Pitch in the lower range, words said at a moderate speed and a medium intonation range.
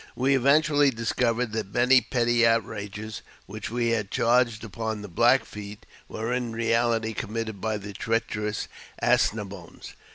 No: low, 115 Hz; average, 150 wpm; narrow, 2.1 semitones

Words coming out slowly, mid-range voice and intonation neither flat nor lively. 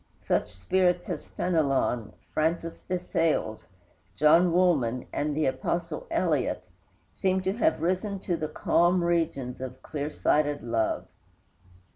Yes: slow, 125 wpm; medium, 165 Hz; average, 4.9 semitones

